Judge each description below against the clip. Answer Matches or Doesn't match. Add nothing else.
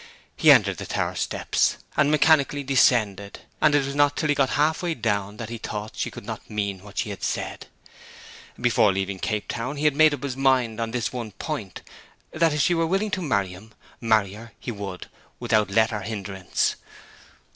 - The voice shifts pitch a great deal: Matches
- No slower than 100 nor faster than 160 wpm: Doesn't match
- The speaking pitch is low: Matches